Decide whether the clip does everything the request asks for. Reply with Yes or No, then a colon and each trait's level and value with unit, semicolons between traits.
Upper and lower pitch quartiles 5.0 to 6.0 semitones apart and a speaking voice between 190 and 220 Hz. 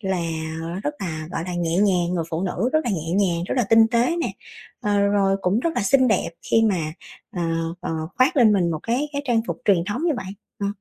Yes: average, 5.3 semitones; high, 200 Hz